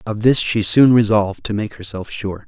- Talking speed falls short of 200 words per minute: No, fast, 220 wpm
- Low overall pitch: Yes, low, 110 Hz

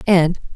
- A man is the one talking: No, female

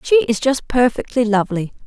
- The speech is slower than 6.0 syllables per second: Yes, 5.5 syllables/s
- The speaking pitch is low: No, high, 240 Hz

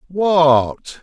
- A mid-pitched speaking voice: Yes, medium, 160 Hz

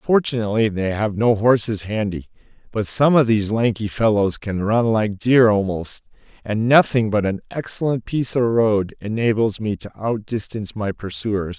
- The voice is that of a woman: No, male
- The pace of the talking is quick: No, average, 160 wpm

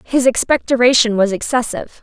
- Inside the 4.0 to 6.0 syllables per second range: Yes, 5.7 syllables/s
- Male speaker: No, female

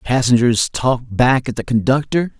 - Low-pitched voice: Yes, low, 125 Hz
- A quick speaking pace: No, average, 150 wpm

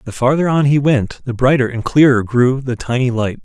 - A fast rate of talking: Yes, fast, 225 wpm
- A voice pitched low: Yes, low, 130 Hz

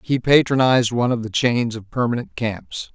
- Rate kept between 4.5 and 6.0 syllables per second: Yes, 5.3 syllables/s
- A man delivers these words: Yes, male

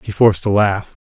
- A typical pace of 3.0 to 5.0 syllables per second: No, 5.7 syllables/s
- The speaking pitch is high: No, low, 100 Hz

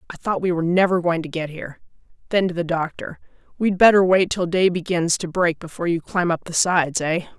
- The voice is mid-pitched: Yes, medium, 175 Hz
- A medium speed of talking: No, fast, 225 wpm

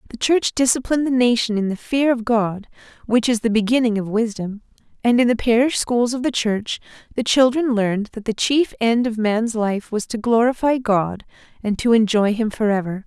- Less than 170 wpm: No, average, 200 wpm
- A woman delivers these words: Yes, female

